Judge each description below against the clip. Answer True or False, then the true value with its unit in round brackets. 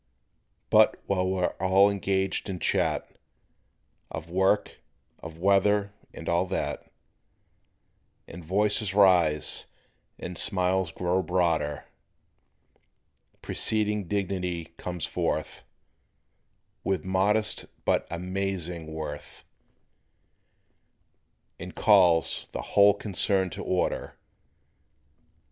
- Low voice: True (95 Hz)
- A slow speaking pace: True (85 wpm)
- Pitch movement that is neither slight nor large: False (2.3 semitones)